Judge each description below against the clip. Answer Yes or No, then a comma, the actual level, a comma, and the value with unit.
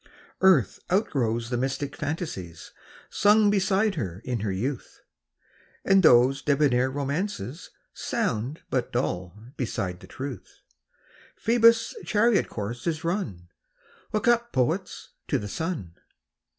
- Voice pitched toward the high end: No, medium, 140 Hz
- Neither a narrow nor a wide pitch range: No, wide, 8.5 semitones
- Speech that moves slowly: Yes, slow, 120 wpm